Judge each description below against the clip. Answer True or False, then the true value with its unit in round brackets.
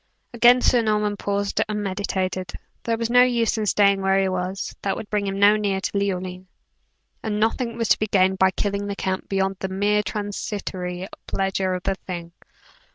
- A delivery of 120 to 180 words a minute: False (190 wpm)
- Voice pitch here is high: True (200 Hz)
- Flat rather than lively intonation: True (1.8 semitones)